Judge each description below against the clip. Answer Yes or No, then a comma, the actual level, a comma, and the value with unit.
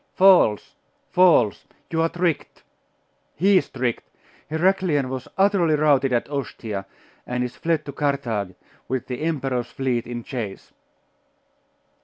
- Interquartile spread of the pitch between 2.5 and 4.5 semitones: No, average, 5.2 semitones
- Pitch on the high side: No, low, 135 Hz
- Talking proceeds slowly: Yes, slow, 125 wpm